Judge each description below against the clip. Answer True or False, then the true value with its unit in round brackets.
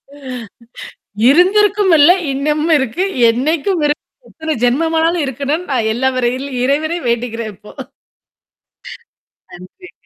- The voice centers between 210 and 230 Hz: False (295 Hz)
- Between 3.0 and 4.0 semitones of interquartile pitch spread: False (5.2 semitones)